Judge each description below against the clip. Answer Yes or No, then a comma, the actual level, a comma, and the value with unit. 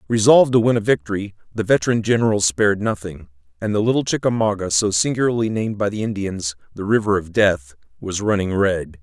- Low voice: Yes, low, 100 Hz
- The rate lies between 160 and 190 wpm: Yes, average, 180 wpm